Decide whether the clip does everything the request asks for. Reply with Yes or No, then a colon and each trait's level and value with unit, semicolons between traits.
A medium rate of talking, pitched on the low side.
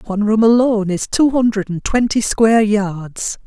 No: average, 175 wpm; high, 215 Hz